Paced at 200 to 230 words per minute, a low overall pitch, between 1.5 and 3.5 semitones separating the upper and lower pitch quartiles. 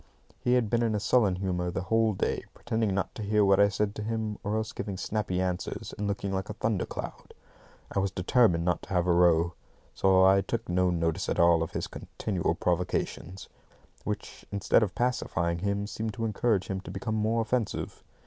Yes: fast, 205 wpm; low, 100 Hz; average, 3.2 semitones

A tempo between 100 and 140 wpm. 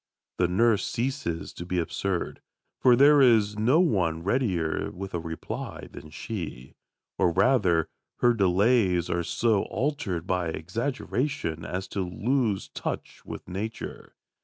Yes: slow, 135 wpm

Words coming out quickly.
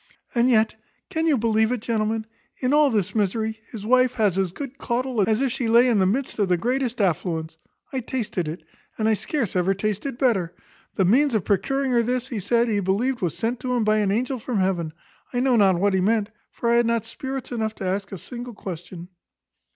Yes: fast, 220 wpm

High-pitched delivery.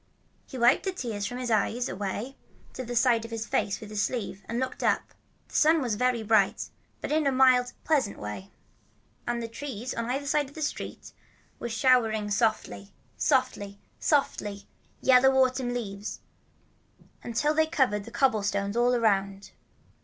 Yes: high, 235 Hz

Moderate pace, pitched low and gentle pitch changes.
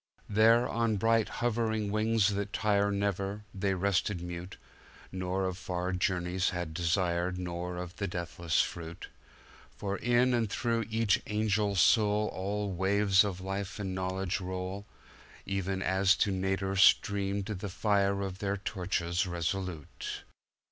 No: slow, 125 wpm; very low, 95 Hz; narrow, 2.2 semitones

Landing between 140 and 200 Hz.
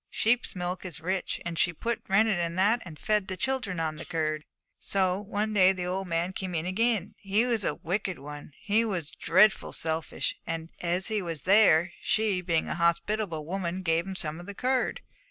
Yes: medium, 185 Hz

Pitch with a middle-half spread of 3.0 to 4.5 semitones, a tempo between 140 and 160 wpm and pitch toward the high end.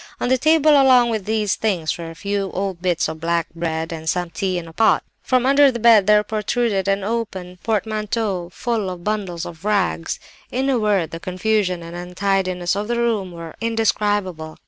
No: average, 4.2 semitones; average, 190 wpm; high, 200 Hz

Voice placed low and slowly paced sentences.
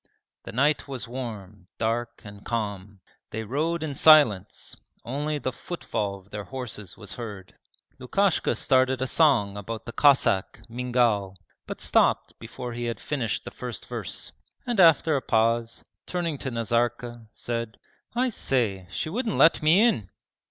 No: low, 120 Hz; average, 150 wpm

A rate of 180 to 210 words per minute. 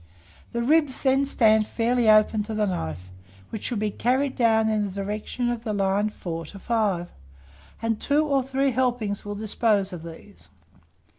No: average, 170 wpm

